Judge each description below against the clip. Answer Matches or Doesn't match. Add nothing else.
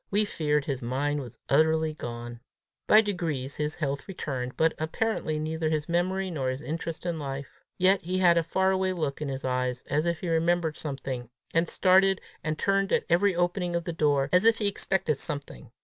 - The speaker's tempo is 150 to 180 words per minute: Doesn't match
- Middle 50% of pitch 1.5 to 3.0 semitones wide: Doesn't match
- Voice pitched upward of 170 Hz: Doesn't match